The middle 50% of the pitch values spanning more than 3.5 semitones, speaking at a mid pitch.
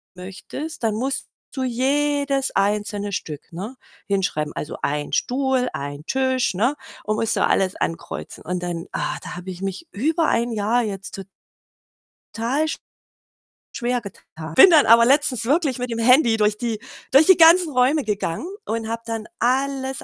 No: average, 5.1 semitones; high, 230 Hz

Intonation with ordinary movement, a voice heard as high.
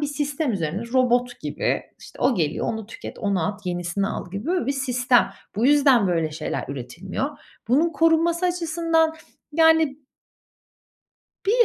No: wide, 8.3 semitones; very high, 255 Hz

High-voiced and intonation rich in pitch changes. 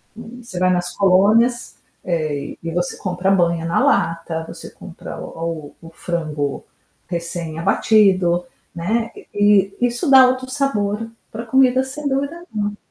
Yes: high, 195 Hz; wide, 5.7 semitones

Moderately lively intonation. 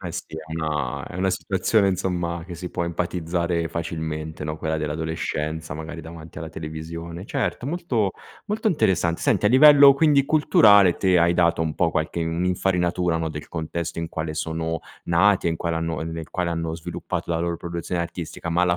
No: narrow, 2.0 semitones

